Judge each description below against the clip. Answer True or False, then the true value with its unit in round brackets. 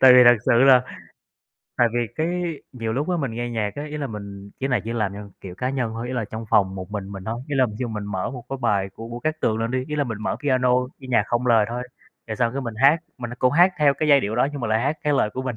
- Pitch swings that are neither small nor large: True (3.6 semitones)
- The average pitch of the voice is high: False (120 Hz)